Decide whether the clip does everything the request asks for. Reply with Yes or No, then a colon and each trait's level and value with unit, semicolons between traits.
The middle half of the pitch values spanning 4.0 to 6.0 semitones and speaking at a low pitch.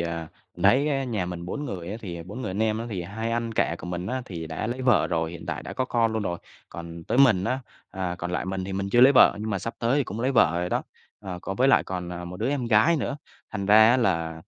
Yes: wide, 5.4 semitones; low, 100 Hz